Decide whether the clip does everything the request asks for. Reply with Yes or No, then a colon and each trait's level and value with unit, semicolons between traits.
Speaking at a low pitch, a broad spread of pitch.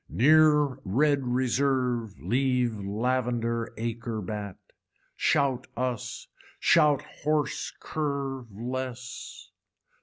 No: low, 125 Hz; average, 3.0 semitones